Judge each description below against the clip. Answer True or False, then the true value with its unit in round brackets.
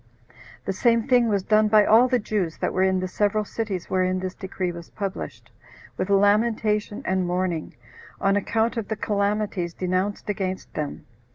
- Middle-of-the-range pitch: False (200 Hz)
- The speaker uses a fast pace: False (170 wpm)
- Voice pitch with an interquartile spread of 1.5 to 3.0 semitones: True (2.5 semitones)